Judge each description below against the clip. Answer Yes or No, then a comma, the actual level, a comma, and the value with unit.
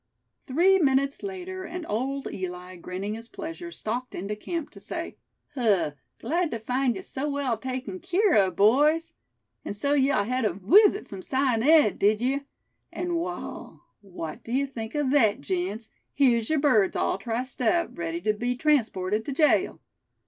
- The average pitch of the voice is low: No, very high, 255 Hz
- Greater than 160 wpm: Yes, average, 170 wpm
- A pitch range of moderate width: No, wide, 6.2 semitones